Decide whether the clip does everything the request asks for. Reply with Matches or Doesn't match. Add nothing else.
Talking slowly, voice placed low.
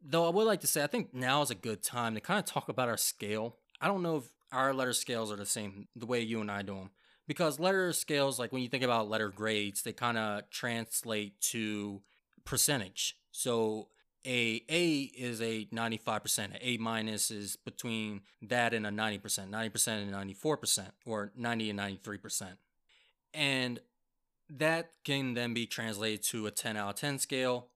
Doesn't match